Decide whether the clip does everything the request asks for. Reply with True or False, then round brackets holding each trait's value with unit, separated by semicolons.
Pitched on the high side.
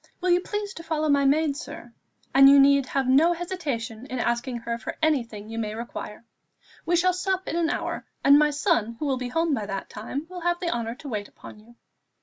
True (280 Hz)